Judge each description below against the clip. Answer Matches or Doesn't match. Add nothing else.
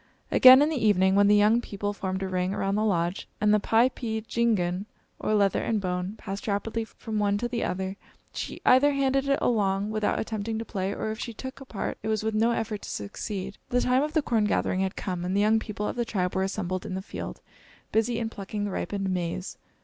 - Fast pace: Matches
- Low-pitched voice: Doesn't match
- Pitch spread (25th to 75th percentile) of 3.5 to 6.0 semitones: Doesn't match